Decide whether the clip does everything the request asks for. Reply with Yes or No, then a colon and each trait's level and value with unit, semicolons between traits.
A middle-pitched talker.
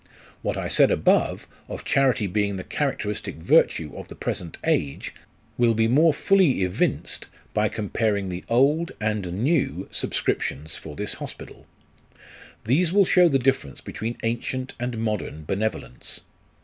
No: low, 110 Hz